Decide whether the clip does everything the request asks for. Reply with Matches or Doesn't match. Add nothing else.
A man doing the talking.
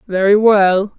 Doesn't match